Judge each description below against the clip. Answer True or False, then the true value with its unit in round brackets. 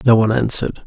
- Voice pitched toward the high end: False (115 Hz)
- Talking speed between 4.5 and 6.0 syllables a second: False (7.8 syllables/s)